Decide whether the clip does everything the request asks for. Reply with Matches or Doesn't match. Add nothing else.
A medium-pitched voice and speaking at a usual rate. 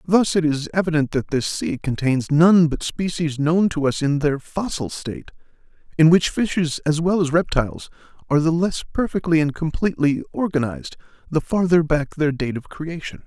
Matches